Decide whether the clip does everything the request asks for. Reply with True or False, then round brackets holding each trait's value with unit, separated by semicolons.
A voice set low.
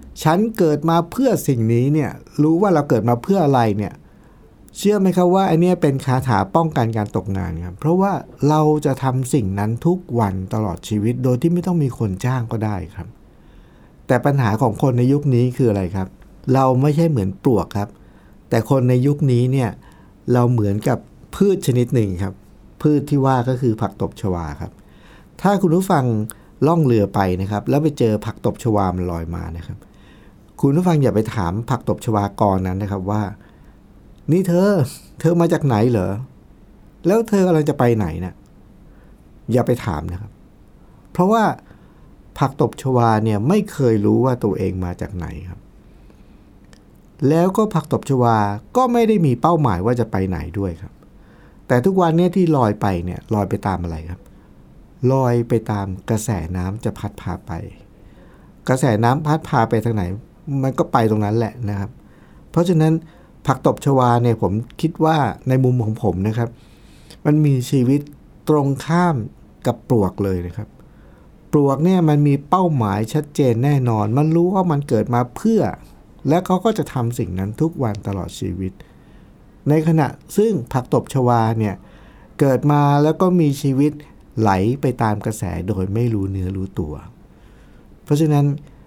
True (125 Hz)